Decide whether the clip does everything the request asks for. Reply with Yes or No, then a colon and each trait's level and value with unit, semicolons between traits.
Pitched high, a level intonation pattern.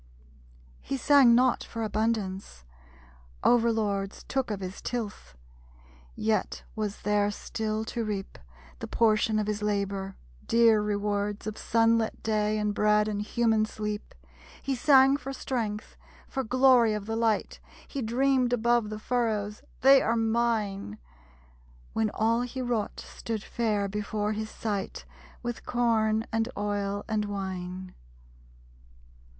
Yes: high, 215 Hz; narrow, 2.2 semitones